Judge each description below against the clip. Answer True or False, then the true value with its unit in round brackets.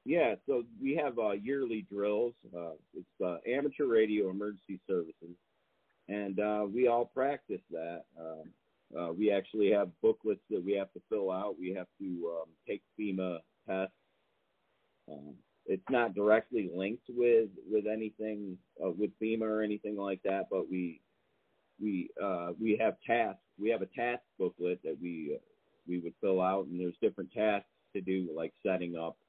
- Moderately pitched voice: False (100 Hz)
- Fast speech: False (170 wpm)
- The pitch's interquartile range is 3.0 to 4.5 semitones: True (3.4 semitones)